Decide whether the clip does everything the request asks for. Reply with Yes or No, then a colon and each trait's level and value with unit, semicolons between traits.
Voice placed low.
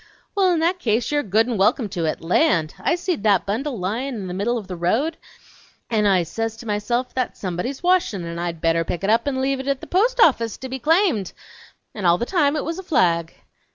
No: high, 230 Hz